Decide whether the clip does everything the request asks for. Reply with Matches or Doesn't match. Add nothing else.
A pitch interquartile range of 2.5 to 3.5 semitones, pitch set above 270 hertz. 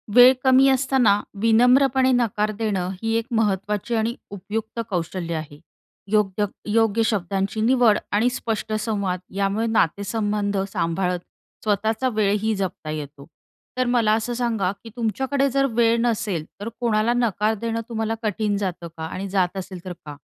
Doesn't match